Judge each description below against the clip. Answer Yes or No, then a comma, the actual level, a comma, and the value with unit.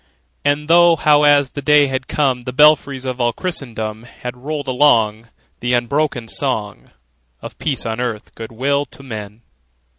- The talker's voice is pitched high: No, low, 130 Hz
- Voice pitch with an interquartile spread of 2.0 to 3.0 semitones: No, average, 3.9 semitones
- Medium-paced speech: Yes, average, 160 wpm